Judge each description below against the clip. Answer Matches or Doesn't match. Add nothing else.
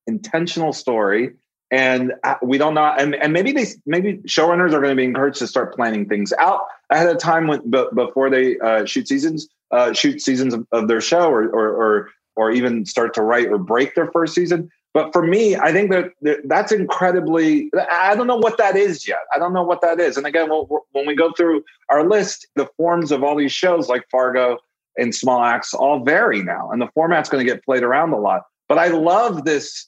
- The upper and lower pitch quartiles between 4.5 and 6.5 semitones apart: Matches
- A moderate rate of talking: Doesn't match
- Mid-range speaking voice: Matches